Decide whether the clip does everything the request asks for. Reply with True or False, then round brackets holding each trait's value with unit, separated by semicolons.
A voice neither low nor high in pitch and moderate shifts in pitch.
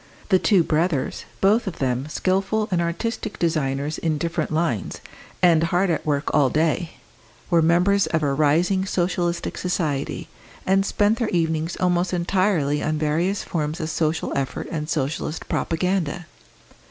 True (170 Hz; 3.3 semitones)